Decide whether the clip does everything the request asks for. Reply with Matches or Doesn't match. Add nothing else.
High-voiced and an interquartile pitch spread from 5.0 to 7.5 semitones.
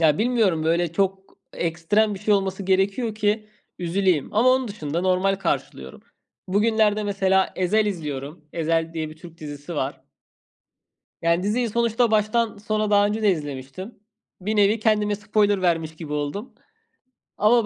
Doesn't match